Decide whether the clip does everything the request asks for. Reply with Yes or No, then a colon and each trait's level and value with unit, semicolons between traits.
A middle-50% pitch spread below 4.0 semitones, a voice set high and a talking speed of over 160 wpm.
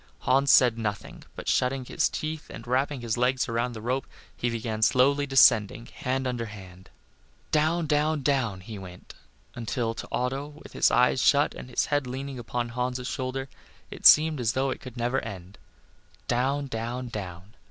No: average, 2.9 semitones; low, 125 Hz; average, 175 wpm